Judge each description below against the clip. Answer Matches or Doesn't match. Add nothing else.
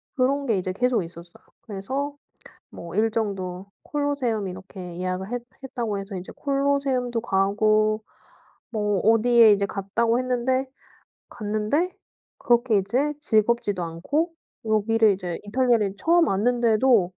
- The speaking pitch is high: Matches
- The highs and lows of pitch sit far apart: Doesn't match